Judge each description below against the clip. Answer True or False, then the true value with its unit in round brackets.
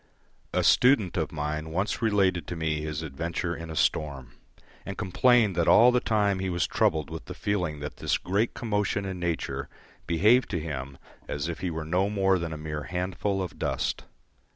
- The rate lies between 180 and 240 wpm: True (190 wpm)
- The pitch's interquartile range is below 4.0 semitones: False (4.3 semitones)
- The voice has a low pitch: True (85 Hz)